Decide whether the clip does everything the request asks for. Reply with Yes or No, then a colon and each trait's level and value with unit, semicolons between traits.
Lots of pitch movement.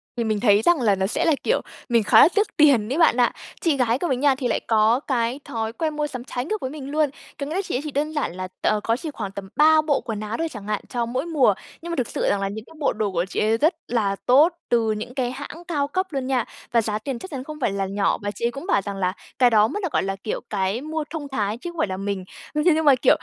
Yes: wide, 6.0 semitones